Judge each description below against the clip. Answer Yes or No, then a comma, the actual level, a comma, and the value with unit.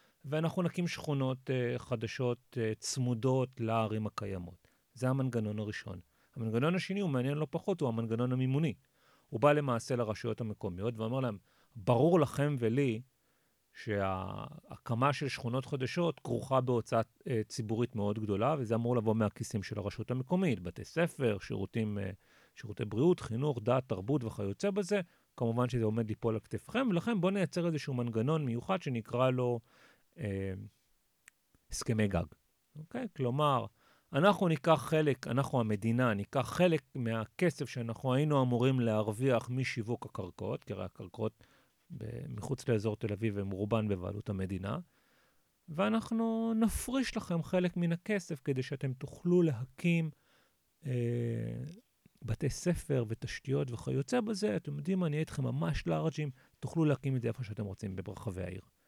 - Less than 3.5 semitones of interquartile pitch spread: No, average, 5.2 semitones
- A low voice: Yes, low, 125 Hz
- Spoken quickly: No, average, 140 wpm